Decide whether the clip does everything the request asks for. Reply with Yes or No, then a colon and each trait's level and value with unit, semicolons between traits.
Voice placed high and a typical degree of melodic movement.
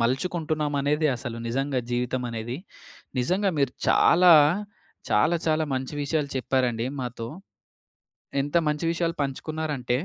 No: medium, 140 Hz; average, 4.1 semitones